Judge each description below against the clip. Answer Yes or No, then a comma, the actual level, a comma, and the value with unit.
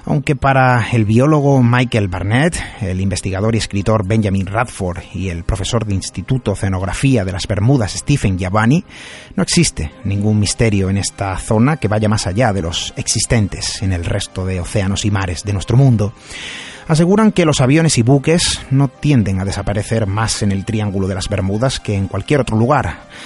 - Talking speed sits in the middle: Yes, average, 180 wpm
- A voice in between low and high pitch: No, low, 110 Hz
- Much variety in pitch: No, average, 4.7 semitones